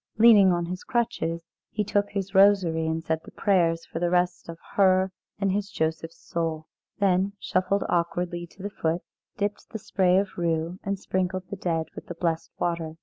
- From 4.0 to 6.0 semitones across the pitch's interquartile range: No, average, 2.9 semitones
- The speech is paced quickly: No, average, 185 wpm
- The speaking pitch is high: No, medium, 180 Hz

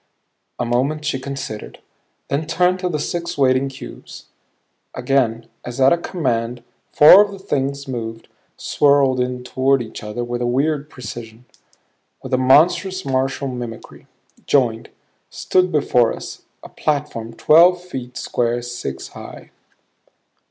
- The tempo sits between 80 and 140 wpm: Yes, slow, 135 wpm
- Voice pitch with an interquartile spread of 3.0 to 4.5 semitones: Yes, average, 3.8 semitones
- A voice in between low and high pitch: No, low, 130 Hz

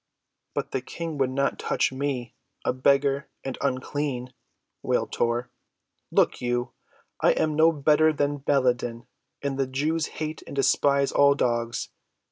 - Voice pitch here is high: No, medium, 140 Hz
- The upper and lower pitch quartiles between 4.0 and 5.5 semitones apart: No, narrow, 2.4 semitones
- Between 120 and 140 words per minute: Yes, slow, 135 wpm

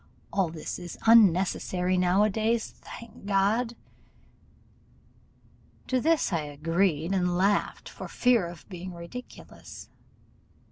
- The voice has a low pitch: No, high, 190 Hz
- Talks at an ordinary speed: No, slow, 110 wpm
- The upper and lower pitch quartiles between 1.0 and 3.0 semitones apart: No, average, 4.1 semitones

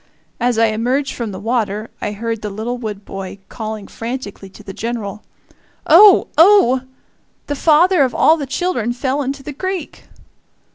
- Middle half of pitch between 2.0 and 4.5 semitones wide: No, average, 4.9 semitones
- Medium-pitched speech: No, high, 240 Hz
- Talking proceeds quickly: No, average, 160 wpm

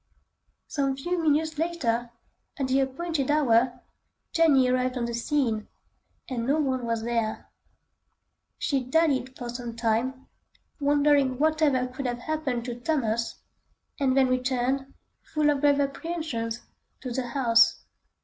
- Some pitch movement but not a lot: Yes, average, 3.3 semitones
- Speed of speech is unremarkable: No, slow, 130 wpm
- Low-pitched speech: No, very high, 260 Hz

